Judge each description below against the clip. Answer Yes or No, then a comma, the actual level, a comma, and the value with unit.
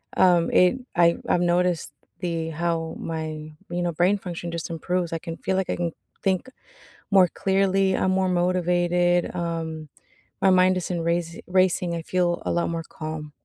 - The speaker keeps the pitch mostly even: Yes, narrow, 1.7 semitones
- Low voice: No, medium, 175 Hz